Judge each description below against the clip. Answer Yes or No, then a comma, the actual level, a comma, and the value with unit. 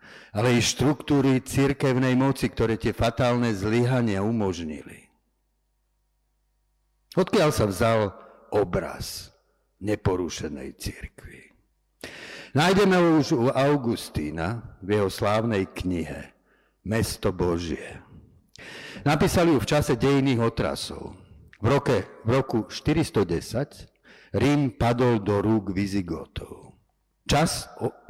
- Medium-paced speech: No, slow, 95 wpm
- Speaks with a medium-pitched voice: No, low, 115 Hz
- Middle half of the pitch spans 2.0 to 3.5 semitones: No, average, 5.0 semitones